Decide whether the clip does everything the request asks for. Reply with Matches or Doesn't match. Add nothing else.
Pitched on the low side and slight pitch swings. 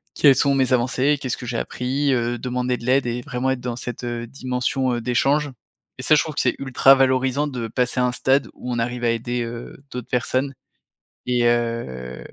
Matches